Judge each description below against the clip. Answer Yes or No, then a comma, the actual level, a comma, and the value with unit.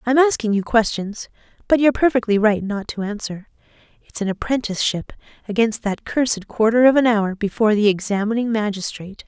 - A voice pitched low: No, high, 220 Hz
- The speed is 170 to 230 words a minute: No, average, 160 wpm